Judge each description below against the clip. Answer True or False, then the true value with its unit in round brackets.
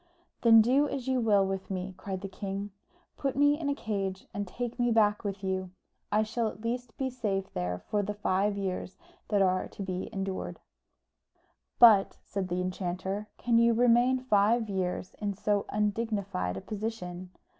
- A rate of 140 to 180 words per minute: True (175 wpm)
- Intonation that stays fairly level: False (3.3 semitones)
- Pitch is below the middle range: False (205 Hz)